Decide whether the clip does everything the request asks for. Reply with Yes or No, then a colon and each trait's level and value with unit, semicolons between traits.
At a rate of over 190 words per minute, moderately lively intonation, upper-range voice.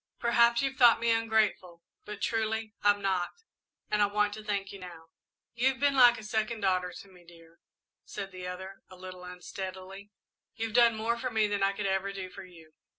Yes: average, 200 wpm; average, 3.4 semitones; high, 205 Hz